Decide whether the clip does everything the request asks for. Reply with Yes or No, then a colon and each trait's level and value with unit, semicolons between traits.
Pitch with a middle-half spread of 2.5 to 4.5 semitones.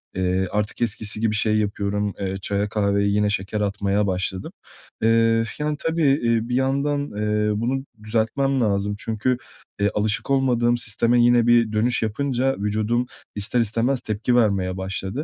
Yes: average, 2.9 semitones